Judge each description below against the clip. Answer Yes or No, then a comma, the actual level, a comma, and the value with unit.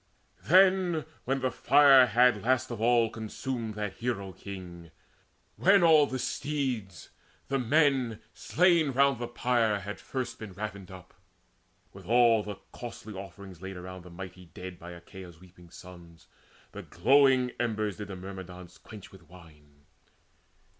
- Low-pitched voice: Yes, low, 110 Hz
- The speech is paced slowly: No, average, 145 wpm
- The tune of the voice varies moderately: No, wide, 5.8 semitones